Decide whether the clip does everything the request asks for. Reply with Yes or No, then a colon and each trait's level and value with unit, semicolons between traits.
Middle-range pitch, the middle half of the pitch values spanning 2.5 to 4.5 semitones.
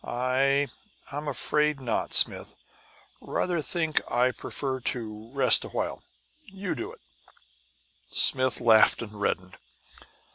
No: low, 130 Hz; average, 4.2 semitones